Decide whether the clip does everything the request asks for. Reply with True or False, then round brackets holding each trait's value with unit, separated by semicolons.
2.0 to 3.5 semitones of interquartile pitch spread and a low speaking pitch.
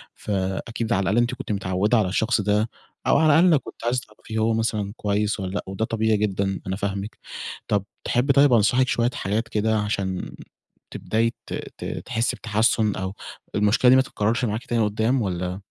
True (2.8 semitones; 110 Hz)